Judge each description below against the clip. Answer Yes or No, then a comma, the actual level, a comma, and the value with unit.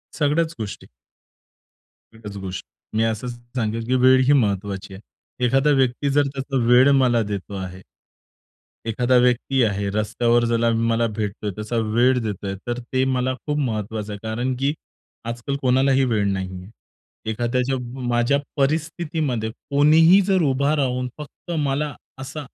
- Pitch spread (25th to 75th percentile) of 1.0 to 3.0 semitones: No, average, 3.8 semitones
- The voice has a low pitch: Yes, low, 120 Hz